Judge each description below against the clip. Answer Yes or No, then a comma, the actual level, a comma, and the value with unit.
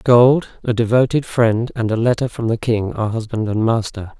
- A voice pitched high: No, low, 115 Hz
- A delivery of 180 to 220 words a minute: Yes, average, 200 wpm